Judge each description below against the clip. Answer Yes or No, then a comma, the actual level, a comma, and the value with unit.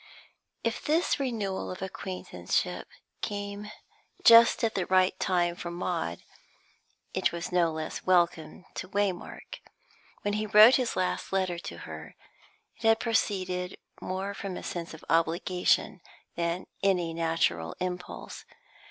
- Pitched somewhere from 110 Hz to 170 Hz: No, medium, 185 Hz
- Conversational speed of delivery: No, slow, 130 wpm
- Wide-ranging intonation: No, average, 2.9 semitones